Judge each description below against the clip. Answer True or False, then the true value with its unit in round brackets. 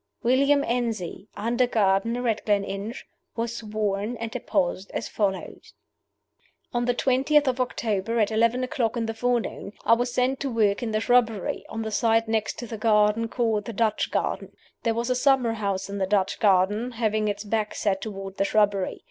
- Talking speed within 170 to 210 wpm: True (180 wpm)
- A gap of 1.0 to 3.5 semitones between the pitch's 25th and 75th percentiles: True (2.7 semitones)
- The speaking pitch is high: True (225 Hz)